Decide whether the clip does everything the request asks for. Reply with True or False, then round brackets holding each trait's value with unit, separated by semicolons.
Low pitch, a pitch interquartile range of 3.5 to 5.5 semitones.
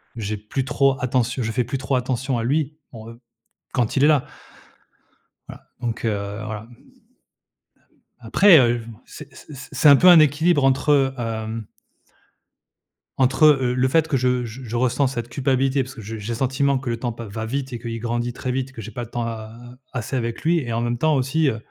False (125 Hz; 2.8 semitones)